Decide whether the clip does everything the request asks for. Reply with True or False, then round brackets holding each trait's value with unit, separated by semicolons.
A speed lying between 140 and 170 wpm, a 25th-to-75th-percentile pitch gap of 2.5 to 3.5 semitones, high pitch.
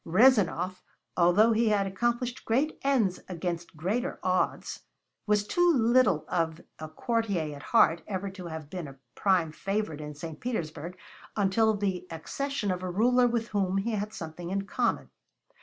False (155 wpm; 5.0 semitones; 195 Hz)